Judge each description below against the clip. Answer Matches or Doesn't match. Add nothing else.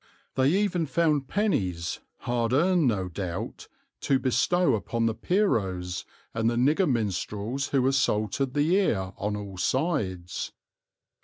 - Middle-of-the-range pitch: Doesn't match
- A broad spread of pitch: Matches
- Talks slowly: Matches